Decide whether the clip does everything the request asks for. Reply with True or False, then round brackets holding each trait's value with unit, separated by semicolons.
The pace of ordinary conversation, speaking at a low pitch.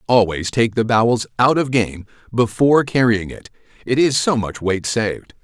True (175 wpm; 115 Hz)